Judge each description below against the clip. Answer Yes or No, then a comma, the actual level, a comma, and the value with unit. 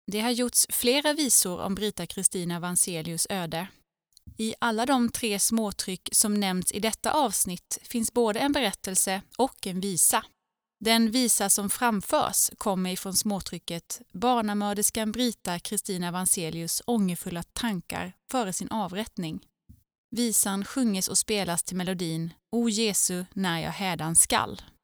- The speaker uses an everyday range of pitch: Yes, average, 3.9 semitones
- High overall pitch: Yes, high, 200 Hz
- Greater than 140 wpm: No, average, 135 wpm